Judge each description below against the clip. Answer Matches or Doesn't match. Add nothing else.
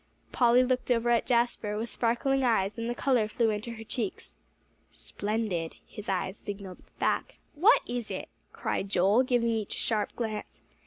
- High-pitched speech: Matches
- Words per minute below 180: Matches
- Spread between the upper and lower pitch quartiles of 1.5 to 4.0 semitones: Matches